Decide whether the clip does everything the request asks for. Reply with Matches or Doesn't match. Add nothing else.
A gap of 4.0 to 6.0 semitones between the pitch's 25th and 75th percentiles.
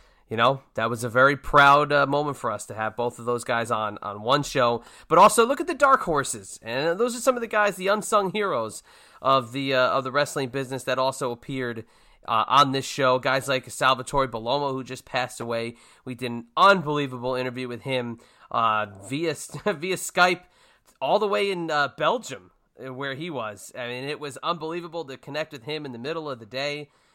Matches